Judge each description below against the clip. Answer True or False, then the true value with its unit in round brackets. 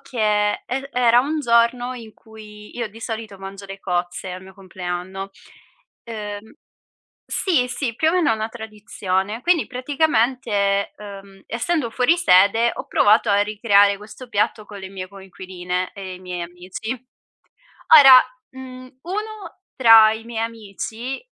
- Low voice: False (220 Hz)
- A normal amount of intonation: True (4.0 semitones)